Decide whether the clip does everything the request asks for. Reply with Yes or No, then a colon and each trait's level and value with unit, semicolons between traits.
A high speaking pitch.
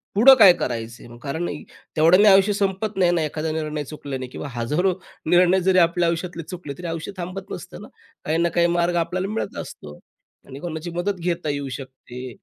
No: medium, 170 Hz